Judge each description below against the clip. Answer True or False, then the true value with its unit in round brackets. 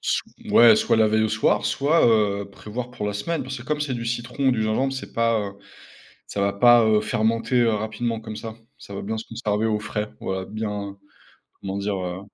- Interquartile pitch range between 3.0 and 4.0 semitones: False (2.4 semitones)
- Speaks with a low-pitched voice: True (110 Hz)